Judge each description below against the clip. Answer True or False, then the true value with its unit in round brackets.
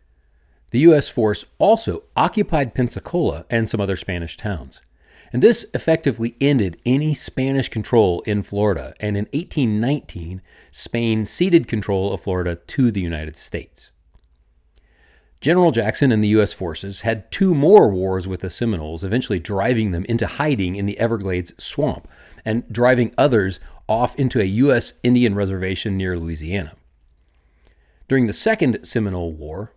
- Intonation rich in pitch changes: True (6.0 semitones)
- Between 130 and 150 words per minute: True (140 wpm)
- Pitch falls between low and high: False (105 Hz)